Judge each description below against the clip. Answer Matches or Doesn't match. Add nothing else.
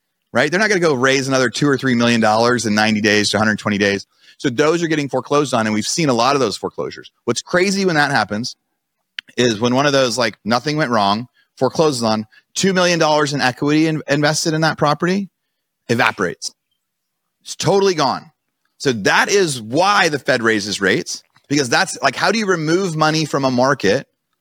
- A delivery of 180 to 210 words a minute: Matches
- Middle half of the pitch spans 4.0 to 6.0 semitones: Matches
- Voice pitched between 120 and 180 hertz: Matches